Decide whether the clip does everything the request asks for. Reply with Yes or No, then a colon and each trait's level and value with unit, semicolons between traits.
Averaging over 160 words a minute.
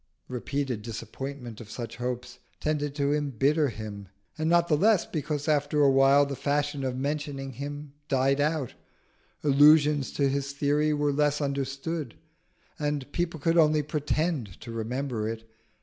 No: average, 150 wpm